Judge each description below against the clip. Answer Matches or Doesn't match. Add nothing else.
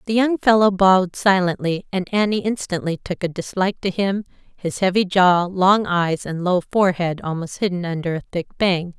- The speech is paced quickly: Doesn't match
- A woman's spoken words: Matches